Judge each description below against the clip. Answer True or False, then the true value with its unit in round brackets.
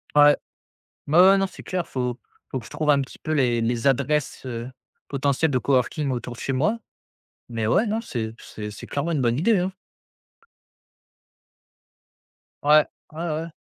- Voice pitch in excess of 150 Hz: False (140 Hz)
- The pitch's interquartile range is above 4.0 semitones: True (4.4 semitones)